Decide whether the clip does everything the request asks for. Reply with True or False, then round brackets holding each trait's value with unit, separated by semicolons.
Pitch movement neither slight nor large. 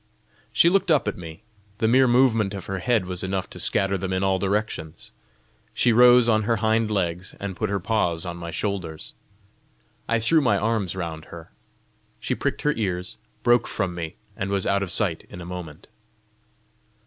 True (4.1 semitones)